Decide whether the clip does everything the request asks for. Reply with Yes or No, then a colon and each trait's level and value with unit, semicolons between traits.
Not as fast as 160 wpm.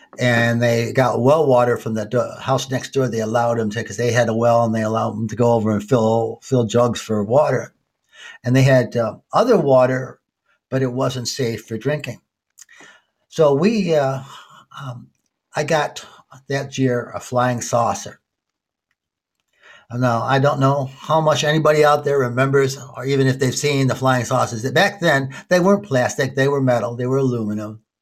No: average, 180 wpm